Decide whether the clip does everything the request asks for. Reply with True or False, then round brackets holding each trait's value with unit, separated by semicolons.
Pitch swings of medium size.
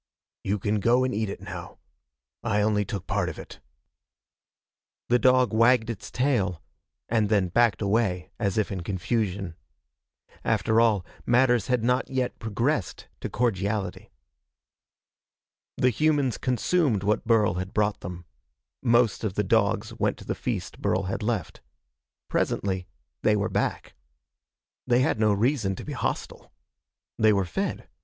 True (3.5 semitones)